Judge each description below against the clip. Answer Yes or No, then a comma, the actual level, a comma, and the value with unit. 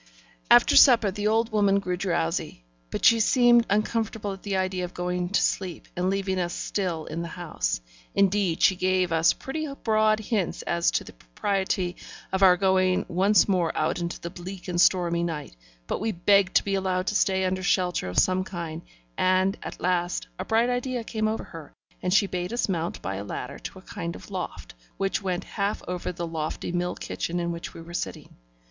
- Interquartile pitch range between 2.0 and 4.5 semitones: Yes, narrow, 2.6 semitones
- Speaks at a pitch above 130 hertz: Yes, medium, 185 Hz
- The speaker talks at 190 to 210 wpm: Yes, average, 200 wpm